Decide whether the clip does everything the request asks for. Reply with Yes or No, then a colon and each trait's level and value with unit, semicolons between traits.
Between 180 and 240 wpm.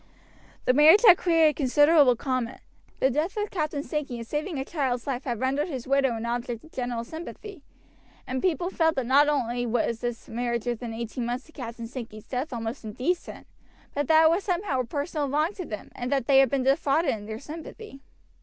Yes: average, 200 wpm